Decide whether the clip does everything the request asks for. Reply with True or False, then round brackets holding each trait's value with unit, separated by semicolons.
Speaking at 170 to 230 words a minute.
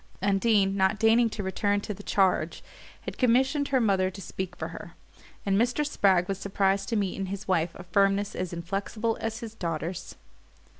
True (185 wpm)